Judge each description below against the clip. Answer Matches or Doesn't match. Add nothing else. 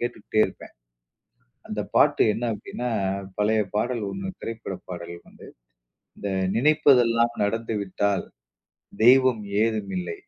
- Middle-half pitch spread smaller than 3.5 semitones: Matches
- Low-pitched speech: Matches